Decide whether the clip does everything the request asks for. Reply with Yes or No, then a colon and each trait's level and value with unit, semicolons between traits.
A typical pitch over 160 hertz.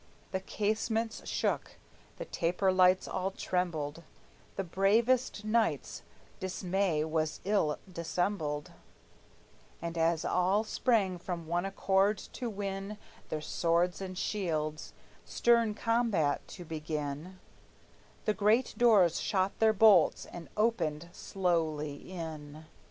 Yes: medium, 185 Hz